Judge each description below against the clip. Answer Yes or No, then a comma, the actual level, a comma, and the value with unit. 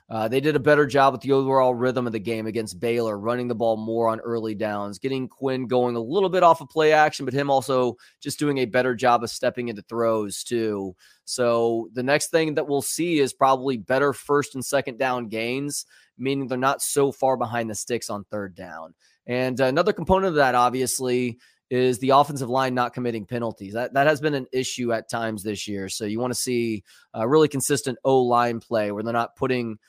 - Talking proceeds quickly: Yes, fast, 220 wpm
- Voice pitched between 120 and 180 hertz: Yes, low, 125 Hz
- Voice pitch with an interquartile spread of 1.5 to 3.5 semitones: Yes, average, 2.9 semitones